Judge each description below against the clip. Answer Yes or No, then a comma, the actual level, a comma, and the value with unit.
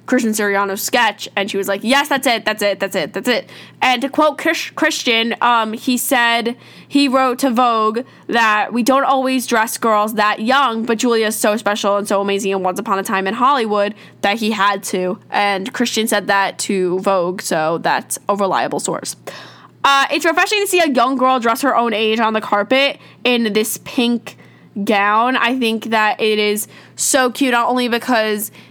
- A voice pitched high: Yes, high, 225 Hz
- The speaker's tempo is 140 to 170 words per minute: No, average, 200 wpm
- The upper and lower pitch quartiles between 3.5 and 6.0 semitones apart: Yes, average, 3.8 semitones